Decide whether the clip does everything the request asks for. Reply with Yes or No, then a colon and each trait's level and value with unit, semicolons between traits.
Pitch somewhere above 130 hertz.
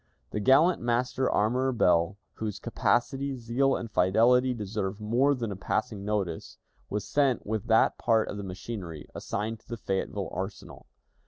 No: low, 110 Hz